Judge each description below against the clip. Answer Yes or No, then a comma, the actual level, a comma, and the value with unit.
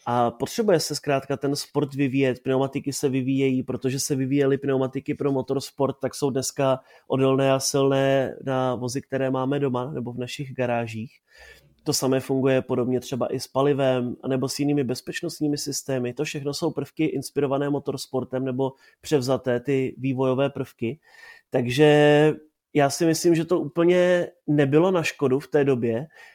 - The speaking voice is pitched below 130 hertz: No, low, 135 Hz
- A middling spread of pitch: No, narrow, 2.0 semitones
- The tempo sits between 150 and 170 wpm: Yes, average, 155 wpm